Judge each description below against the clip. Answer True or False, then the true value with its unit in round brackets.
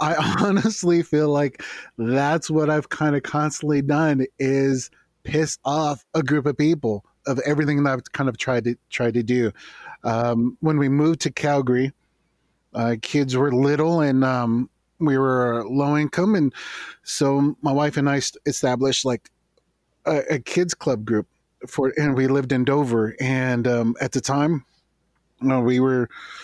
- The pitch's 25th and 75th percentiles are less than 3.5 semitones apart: True (3.0 semitones)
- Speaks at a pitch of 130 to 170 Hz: True (140 Hz)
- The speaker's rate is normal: True (170 wpm)